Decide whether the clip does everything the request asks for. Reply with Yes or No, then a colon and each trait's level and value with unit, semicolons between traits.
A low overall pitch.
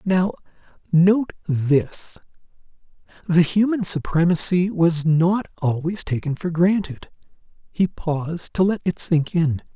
No: medium, 170 Hz